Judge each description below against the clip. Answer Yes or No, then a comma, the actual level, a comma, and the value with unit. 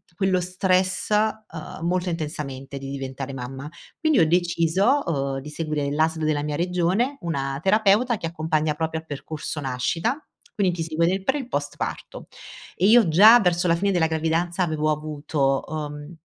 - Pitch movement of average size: Yes, average, 3.8 semitones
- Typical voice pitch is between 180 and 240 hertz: No, medium, 165 Hz